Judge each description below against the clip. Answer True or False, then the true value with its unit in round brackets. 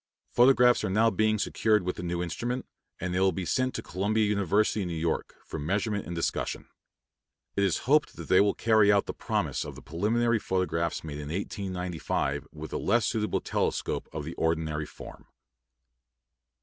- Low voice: True (95 Hz)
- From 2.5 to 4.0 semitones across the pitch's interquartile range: False (4.4 semitones)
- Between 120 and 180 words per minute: True (175 wpm)